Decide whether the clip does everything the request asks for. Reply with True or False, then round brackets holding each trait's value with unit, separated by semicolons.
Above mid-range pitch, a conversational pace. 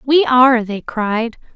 True (245 Hz; 155 wpm)